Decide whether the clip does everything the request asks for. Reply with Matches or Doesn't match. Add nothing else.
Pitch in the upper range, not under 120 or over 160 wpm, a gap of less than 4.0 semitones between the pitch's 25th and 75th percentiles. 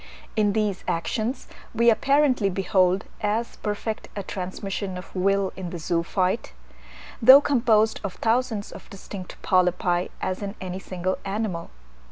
Matches